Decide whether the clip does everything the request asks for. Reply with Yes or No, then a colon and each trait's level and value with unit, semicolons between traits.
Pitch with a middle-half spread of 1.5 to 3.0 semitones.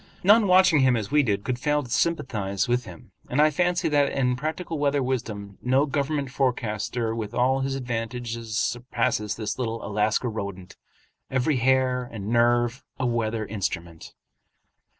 No: average, 3.8 semitones